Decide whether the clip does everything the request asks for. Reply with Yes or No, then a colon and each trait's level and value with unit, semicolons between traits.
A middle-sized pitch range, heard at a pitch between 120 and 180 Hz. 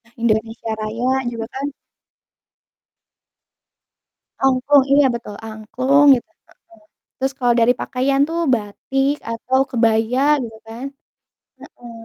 No: average, 3.0 semitones; high, 245 Hz